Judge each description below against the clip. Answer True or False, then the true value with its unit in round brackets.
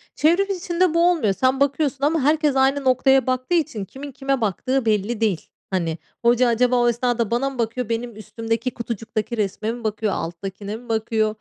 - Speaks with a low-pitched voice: False (240 Hz)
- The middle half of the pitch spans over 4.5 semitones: False (3.7 semitones)